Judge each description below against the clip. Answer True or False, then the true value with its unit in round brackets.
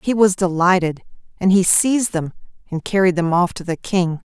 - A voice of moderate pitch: True (180 Hz)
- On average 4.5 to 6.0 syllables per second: True (5.2 syllables/s)